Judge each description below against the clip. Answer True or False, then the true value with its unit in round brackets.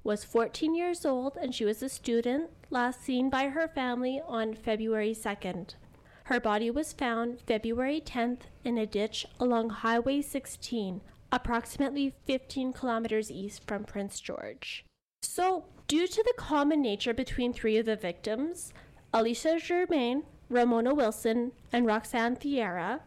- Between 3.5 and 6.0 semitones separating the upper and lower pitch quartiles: True (3.8 semitones)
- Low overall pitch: False (245 Hz)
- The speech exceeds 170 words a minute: False (140 wpm)